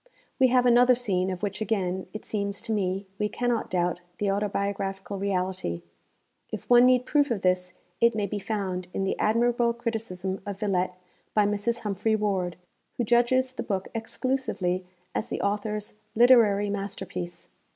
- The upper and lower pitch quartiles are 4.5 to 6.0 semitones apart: No, average, 3.7 semitones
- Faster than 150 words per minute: Yes, average, 160 wpm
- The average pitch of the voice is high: Yes, high, 205 Hz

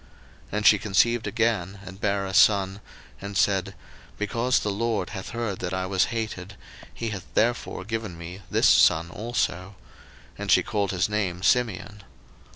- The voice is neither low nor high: No, low, 100 Hz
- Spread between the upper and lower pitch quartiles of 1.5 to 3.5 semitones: Yes, average, 3.1 semitones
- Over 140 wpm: Yes, average, 160 wpm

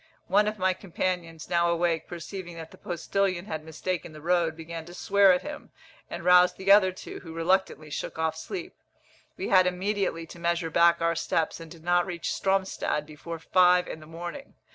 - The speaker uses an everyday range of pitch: No, narrow, 2.1 semitones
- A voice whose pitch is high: No, medium, 175 Hz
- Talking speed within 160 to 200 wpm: Yes, average, 190 wpm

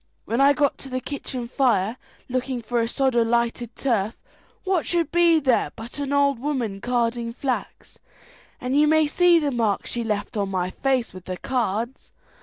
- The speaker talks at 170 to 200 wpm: Yes, average, 185 wpm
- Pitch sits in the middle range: No, very high, 250 Hz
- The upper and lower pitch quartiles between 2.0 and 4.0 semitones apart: Yes, average, 3.5 semitones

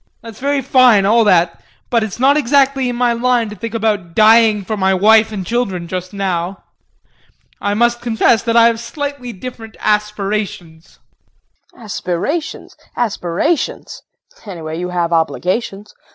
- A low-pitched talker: No, high, 215 Hz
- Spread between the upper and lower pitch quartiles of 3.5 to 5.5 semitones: Yes, average, 4.1 semitones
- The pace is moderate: Yes, average, 150 wpm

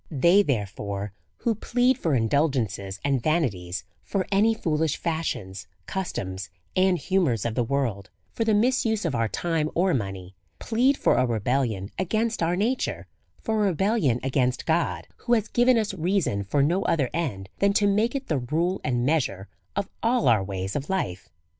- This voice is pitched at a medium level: Yes, medium, 155 Hz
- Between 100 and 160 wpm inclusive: No, average, 175 wpm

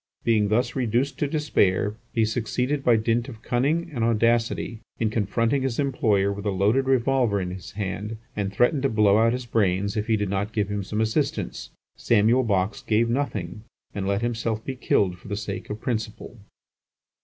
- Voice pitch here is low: Yes, low, 110 Hz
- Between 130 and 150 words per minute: No, average, 185 wpm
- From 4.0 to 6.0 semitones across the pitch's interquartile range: No, average, 3.1 semitones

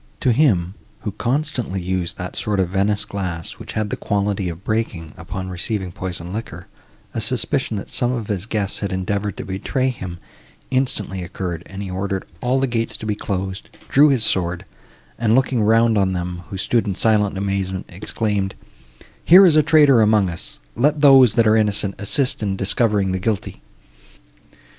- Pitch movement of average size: Yes, average, 3.5 semitones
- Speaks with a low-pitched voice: Yes, low, 100 Hz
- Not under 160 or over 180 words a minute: Yes, average, 175 wpm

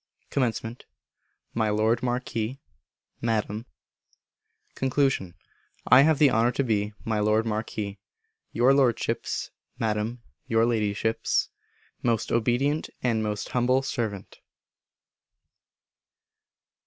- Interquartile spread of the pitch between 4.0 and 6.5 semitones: No, average, 2.8 semitones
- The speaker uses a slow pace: Yes, slow, 90 wpm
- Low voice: Yes, low, 115 Hz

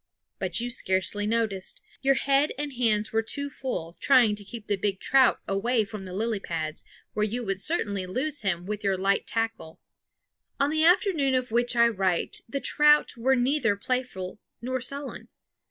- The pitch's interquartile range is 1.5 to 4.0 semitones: No, average, 5.0 semitones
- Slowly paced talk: No, average, 175 wpm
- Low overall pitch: No, high, 225 Hz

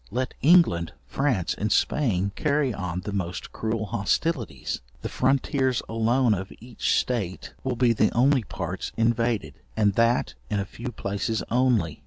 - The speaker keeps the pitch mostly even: No, average, 4.1 semitones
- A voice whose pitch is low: Yes, low, 115 Hz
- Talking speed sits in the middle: Yes, average, 150 wpm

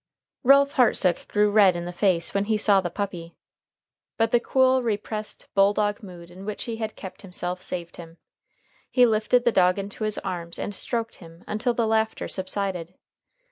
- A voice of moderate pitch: No, high, 205 Hz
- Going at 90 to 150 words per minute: No, average, 180 wpm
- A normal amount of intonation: Yes, average, 3.5 semitones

